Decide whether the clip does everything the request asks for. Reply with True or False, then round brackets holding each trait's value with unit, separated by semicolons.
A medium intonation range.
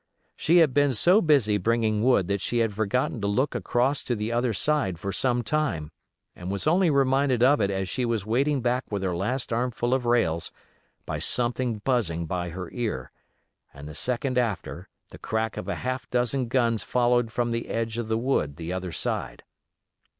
True (4.3 semitones)